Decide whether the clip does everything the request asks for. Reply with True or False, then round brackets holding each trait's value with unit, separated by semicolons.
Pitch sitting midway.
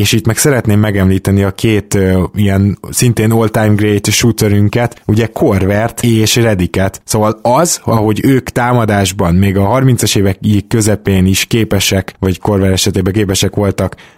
False (105 Hz)